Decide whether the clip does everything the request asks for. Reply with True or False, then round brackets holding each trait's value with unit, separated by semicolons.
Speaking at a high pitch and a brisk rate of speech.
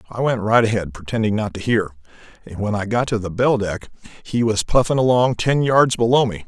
False (110 Hz; 225 wpm)